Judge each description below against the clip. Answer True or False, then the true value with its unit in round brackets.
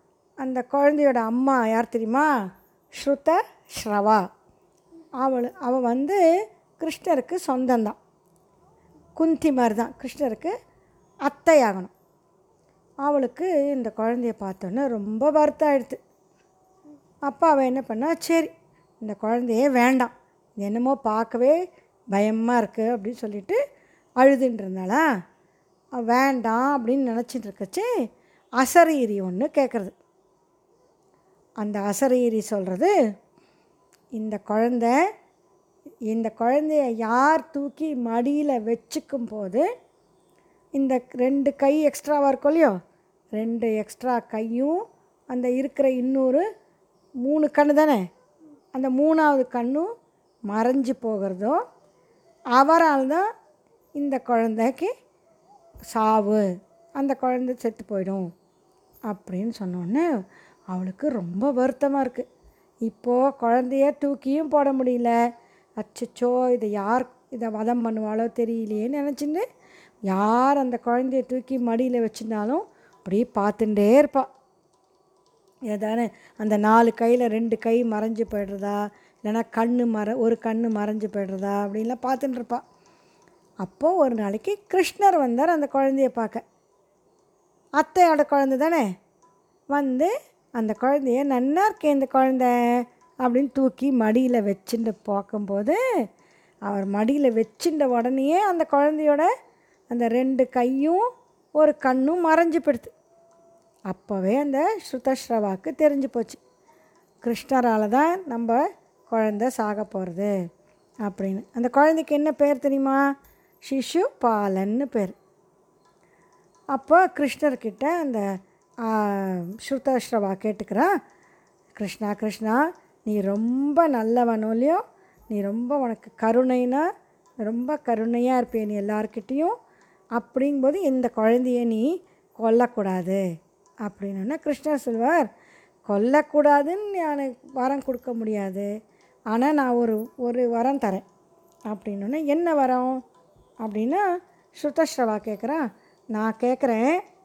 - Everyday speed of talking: True (95 wpm)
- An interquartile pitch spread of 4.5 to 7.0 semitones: True (4.9 semitones)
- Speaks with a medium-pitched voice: False (250 Hz)